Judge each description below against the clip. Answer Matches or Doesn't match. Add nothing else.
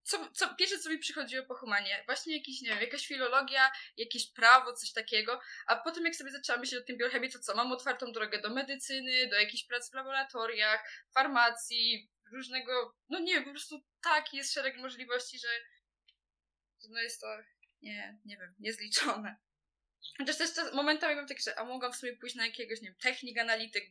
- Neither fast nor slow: Doesn't match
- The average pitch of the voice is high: Matches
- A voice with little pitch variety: Doesn't match